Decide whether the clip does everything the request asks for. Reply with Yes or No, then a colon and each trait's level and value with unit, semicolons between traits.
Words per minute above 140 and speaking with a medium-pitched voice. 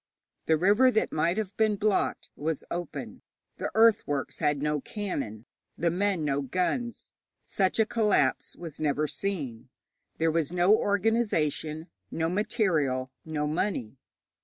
No: slow, 135 wpm; medium, 170 Hz